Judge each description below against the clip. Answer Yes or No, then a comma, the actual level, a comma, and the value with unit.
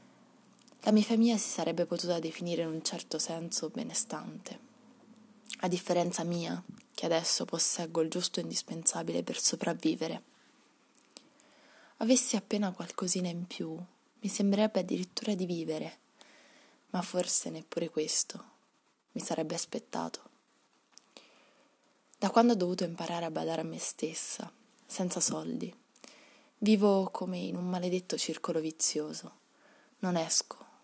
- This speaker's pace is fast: No, average, 120 wpm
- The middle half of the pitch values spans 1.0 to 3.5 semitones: No, wide, 5.4 semitones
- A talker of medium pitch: No, high, 200 Hz